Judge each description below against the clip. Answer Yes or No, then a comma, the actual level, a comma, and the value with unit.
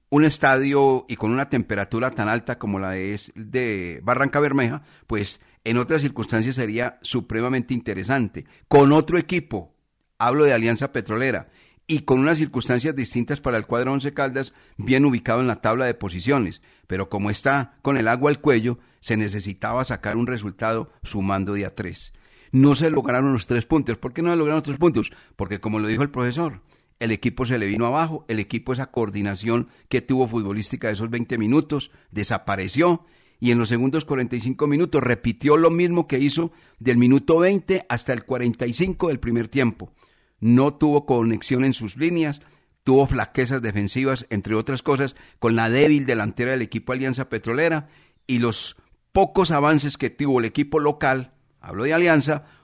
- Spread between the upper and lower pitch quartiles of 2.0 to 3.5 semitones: No, average, 4.2 semitones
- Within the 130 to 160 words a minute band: No, average, 175 wpm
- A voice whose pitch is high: No, low, 125 Hz